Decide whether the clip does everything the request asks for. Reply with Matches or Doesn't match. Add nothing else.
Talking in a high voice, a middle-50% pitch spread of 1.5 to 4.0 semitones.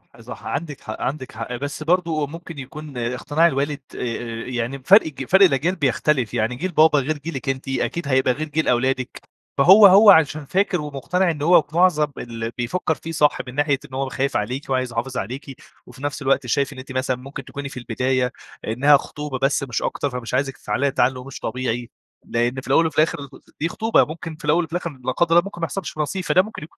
Doesn't match